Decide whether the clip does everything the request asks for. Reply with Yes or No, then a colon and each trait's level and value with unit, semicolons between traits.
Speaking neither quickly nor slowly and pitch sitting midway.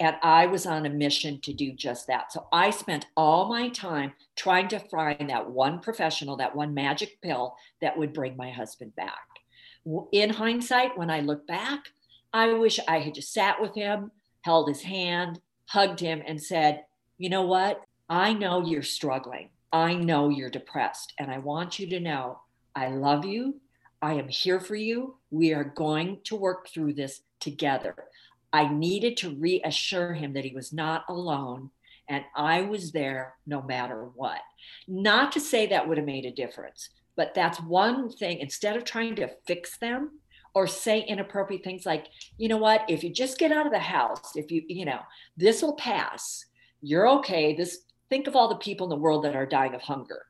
Yes: average, 190 wpm; medium, 165 Hz